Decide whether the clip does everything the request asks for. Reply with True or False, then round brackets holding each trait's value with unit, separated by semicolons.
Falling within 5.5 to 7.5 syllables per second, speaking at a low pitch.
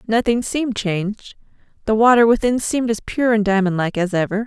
False (5.8 syllables/s; 215 Hz)